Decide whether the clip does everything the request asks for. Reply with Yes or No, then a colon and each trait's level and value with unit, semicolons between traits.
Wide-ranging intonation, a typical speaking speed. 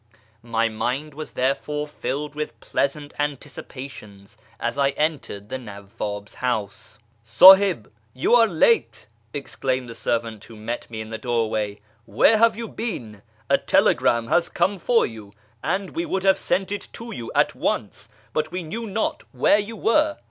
Yes: wide, 8.8 semitones; average, 165 wpm